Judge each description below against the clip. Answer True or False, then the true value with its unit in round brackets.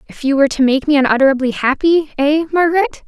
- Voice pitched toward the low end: False (285 Hz)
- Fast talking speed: False (195 wpm)